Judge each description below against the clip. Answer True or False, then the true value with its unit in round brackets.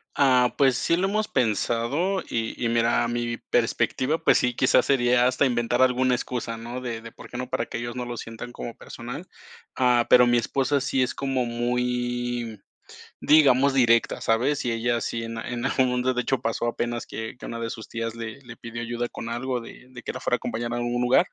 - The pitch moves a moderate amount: False (1.5 semitones)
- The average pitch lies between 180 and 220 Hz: False (120 Hz)